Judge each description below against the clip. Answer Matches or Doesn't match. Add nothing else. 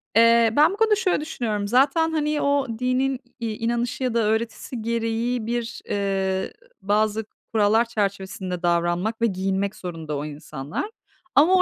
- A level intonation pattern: Doesn't match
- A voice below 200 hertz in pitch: Doesn't match